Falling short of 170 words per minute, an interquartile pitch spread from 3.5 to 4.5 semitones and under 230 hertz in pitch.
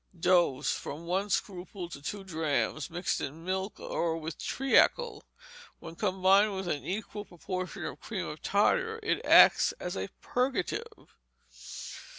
Yes: average, 140 wpm; average, 3.9 semitones; medium, 185 Hz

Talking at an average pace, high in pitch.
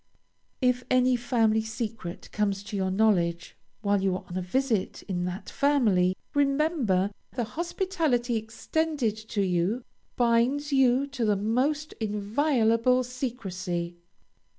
No: slow, 125 wpm; high, 225 Hz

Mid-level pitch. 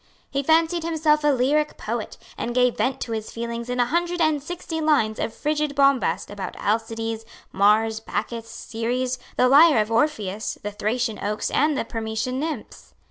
No: very high, 250 Hz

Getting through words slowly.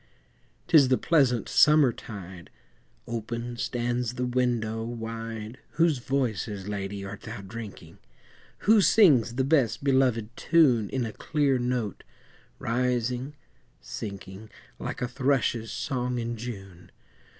Yes: slow, 115 wpm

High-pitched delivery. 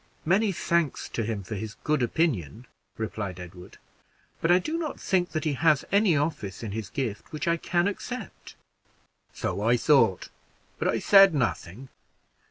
No: medium, 150 Hz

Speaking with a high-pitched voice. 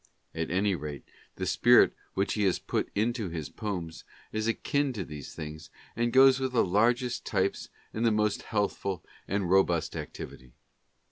No: low, 100 Hz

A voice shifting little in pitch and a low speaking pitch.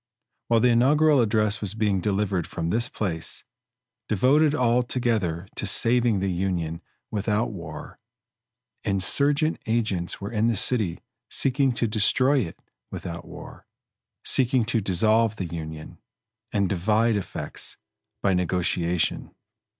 No: average, 4.5 semitones; low, 105 Hz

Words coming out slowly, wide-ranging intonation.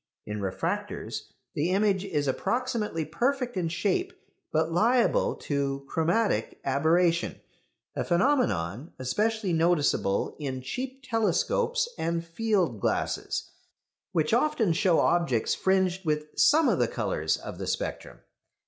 Yes: slow, 120 wpm; wide, 7.0 semitones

